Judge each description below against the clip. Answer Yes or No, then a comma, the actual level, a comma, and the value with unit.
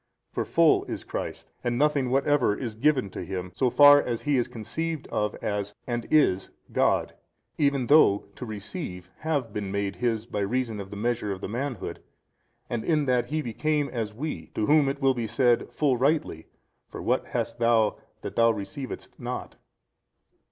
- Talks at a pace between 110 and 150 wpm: No, average, 180 wpm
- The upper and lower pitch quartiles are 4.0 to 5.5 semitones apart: Yes, average, 5.1 semitones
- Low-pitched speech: Yes, low, 120 Hz